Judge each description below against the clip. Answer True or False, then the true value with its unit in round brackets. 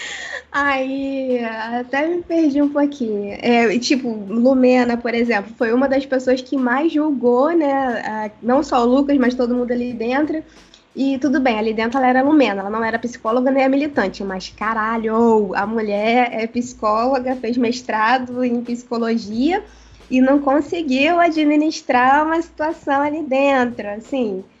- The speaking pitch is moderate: False (255 Hz)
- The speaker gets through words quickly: False (155 wpm)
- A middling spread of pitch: True (3.5 semitones)